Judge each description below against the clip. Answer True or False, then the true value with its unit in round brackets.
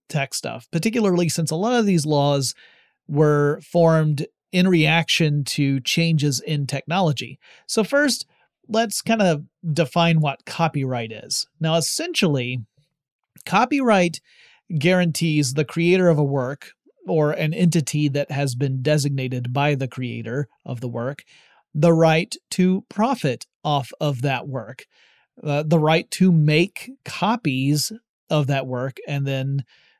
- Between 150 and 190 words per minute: False (135 wpm)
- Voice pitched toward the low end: False (155 Hz)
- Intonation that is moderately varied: True (3.6 semitones)